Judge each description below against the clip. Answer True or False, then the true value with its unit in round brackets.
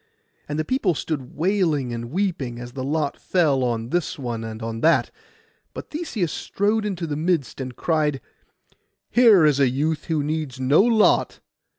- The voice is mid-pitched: True (150 Hz)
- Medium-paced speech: True (165 wpm)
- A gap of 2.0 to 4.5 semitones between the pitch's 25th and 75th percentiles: False (5.5 semitones)